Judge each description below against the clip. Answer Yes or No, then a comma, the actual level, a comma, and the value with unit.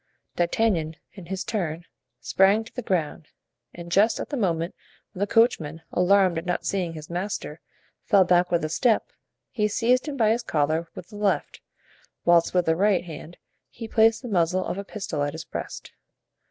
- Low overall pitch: No, medium, 185 Hz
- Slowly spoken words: No, average, 180 wpm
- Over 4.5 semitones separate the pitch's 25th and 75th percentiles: No, average, 4.1 semitones